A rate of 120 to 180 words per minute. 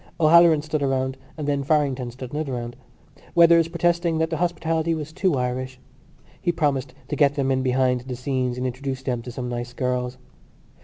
No: average, 190 wpm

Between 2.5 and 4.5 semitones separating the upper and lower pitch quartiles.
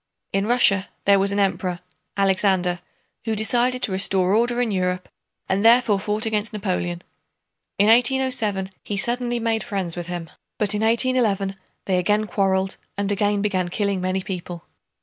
Yes: average, 2.8 semitones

